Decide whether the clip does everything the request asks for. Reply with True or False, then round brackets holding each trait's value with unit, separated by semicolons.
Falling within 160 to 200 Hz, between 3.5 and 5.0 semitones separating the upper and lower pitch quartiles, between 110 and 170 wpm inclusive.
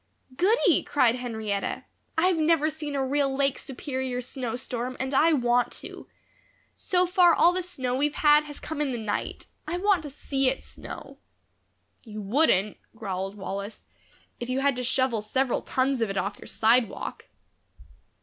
False (260 Hz; 4.3 semitones; 160 wpm)